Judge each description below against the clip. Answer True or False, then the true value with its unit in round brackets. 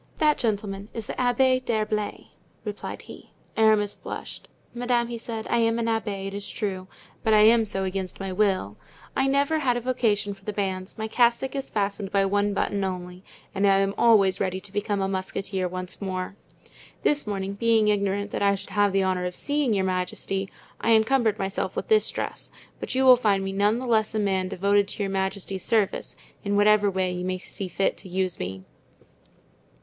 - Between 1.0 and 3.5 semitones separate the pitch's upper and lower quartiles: True (2.8 semitones)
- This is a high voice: True (205 Hz)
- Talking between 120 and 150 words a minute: False (200 wpm)